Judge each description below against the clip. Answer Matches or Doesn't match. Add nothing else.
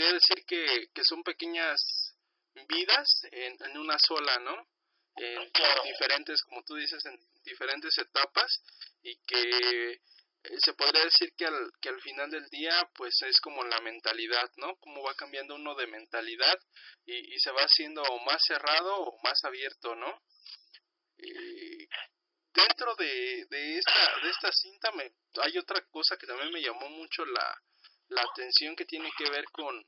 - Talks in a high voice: Matches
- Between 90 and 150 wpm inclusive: Doesn't match